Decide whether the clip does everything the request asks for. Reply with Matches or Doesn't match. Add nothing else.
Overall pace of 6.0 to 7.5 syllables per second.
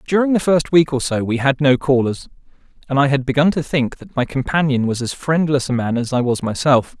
Doesn't match